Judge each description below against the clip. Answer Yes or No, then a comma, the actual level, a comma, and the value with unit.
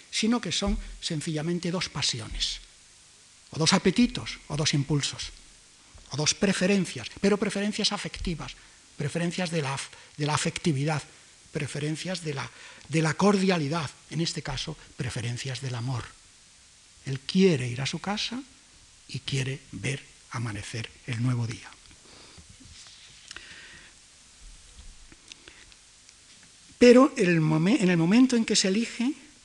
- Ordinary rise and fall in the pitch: No, wide, 6.5 semitones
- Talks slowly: Yes, slow, 115 wpm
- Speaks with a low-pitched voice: No, medium, 155 Hz